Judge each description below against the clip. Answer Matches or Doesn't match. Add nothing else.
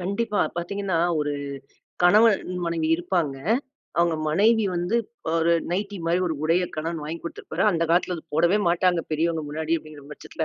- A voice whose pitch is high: Doesn't match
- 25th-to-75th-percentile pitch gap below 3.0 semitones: Matches